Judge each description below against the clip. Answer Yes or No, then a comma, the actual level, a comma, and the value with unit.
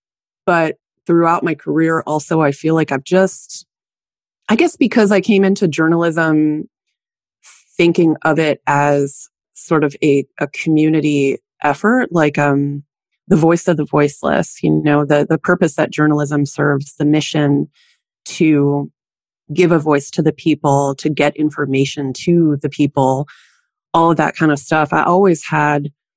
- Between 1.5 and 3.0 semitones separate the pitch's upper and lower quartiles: Yes, average, 2.7 semitones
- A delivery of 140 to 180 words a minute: Yes, average, 150 wpm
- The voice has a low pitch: No, medium, 155 Hz